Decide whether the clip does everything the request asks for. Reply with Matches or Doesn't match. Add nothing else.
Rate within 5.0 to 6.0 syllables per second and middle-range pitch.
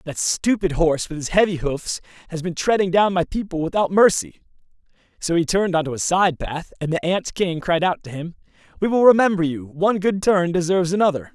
Matches